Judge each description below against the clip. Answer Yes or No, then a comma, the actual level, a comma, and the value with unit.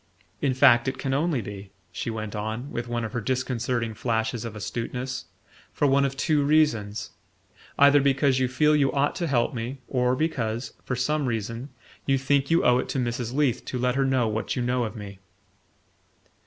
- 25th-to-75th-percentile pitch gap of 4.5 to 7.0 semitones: No, average, 3.2 semitones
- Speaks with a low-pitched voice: Yes, low, 125 Hz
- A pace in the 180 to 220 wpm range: Yes, average, 195 wpm